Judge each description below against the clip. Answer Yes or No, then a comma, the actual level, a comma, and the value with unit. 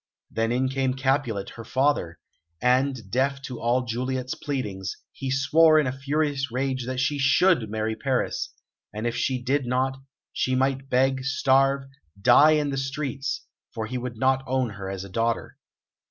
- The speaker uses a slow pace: No, average, 170 wpm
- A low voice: Yes, low, 130 Hz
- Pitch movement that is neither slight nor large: No, narrow, 2.3 semitones